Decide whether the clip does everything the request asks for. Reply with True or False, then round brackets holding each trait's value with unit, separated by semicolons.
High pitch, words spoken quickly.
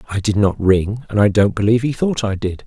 False (105 Hz; 270 wpm)